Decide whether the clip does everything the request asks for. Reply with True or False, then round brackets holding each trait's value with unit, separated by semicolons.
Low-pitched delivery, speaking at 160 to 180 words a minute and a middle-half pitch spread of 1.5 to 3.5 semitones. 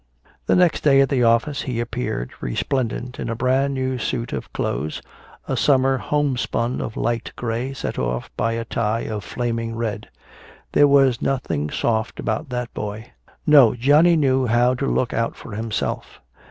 True (120 Hz; 165 wpm; 2.8 semitones)